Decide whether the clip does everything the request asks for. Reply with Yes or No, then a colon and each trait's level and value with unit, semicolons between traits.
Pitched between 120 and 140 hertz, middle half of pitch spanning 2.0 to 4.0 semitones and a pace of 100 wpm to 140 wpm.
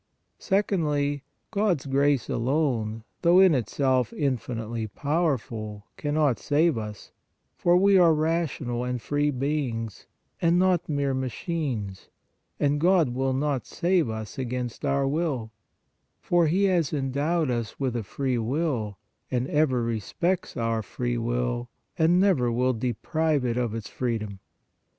No: low, 135 Hz; average, 5.1 semitones; slow, 135 wpm